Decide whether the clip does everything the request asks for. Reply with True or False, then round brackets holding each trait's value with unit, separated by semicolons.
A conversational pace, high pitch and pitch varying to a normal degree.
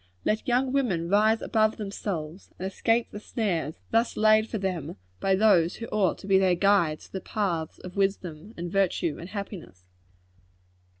True (170 wpm; 195 Hz; 3.9 semitones)